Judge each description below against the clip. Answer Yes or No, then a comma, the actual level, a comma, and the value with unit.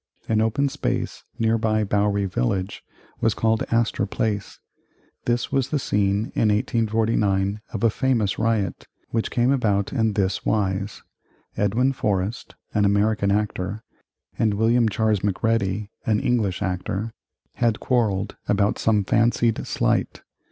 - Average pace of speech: No, slow, 130 wpm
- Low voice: Yes, low, 110 Hz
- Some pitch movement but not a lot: No, narrow, 2.2 semitones